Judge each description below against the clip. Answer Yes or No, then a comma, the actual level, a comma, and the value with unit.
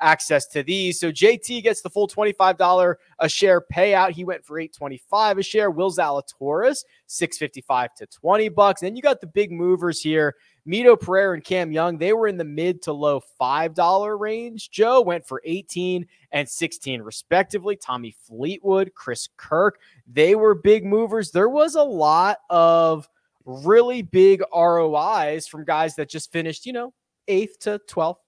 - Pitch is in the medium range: Yes, medium, 180 Hz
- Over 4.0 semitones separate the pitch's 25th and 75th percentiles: Yes, average, 4.7 semitones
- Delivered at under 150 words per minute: No, average, 165 wpm